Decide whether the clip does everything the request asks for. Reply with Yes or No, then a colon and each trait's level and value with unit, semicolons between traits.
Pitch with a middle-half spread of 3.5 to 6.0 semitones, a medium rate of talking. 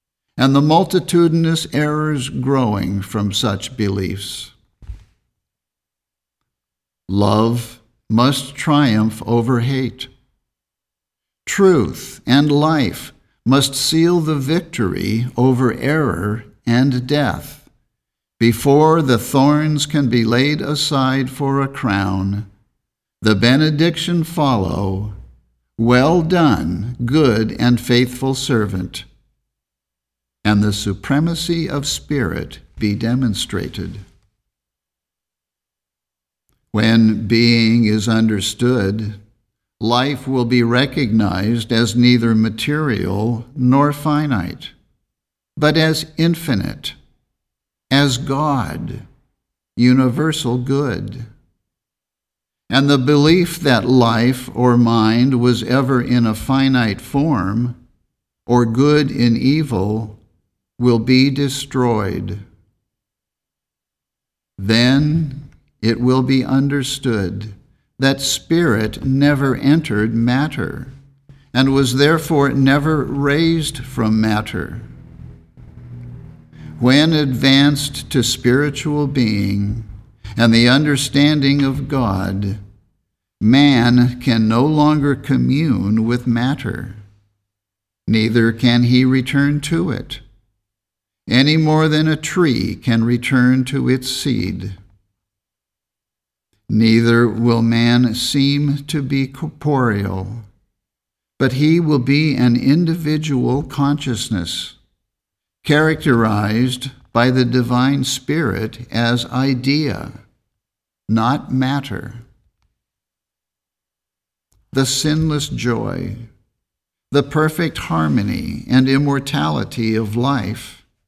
No: average, 4.4 semitones; slow, 85 wpm